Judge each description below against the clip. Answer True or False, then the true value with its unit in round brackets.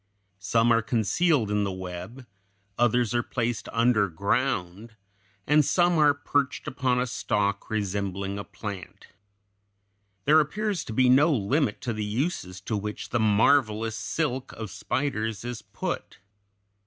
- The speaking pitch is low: True (115 Hz)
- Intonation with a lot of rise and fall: False (4.5 semitones)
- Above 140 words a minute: False (135 wpm)